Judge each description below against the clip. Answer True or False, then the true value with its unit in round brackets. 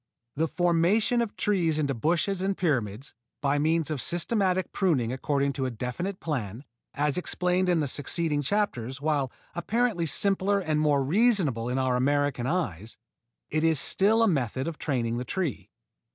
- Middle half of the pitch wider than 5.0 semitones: True (5.6 semitones)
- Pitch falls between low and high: True (155 Hz)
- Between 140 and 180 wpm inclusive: True (160 wpm)